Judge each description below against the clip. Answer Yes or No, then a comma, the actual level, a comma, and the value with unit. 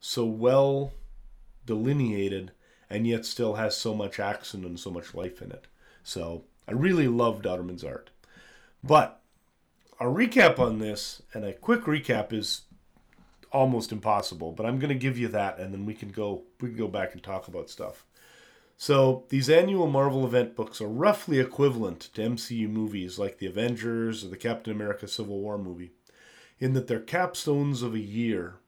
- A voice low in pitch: Yes, low, 115 Hz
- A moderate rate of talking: Yes, average, 175 wpm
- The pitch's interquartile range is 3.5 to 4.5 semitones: Yes, average, 4.2 semitones